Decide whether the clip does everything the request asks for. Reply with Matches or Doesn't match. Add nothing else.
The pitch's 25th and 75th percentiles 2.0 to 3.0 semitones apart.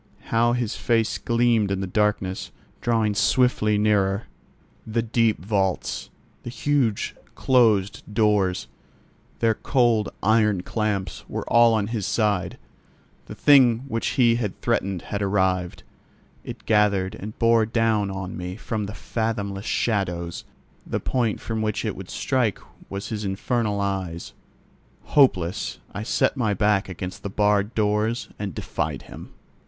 Matches